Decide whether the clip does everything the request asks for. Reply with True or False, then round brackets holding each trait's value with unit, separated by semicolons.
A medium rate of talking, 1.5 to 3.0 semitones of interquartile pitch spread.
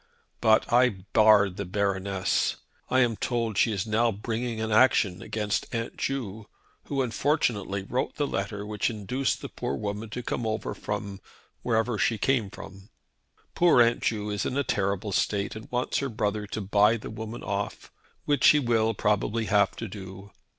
True (170 wpm; 2.7 semitones)